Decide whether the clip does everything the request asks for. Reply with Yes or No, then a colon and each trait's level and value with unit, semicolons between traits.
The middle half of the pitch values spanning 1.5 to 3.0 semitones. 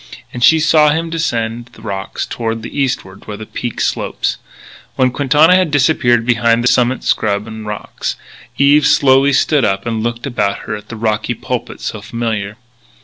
No: average, 4.2 semitones